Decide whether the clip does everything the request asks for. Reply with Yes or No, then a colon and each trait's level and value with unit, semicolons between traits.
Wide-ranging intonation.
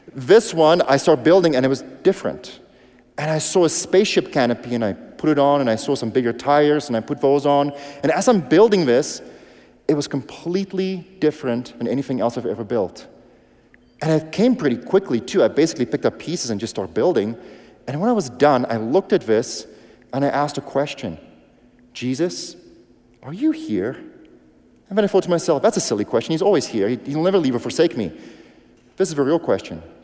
Yes: wide, 6.1 semitones